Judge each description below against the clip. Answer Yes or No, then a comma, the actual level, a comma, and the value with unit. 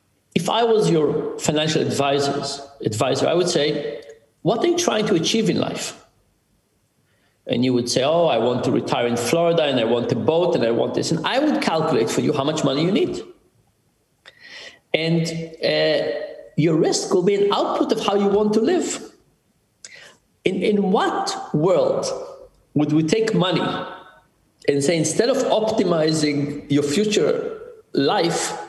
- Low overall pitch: No, medium, 185 Hz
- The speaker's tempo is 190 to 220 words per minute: No, average, 165 wpm